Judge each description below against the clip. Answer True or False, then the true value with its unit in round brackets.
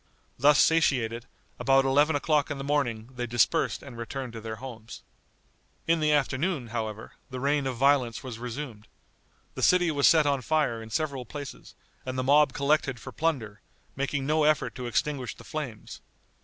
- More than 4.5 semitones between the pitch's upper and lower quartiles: False (3.8 semitones)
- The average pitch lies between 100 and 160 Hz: True (135 Hz)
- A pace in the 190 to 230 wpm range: False (170 wpm)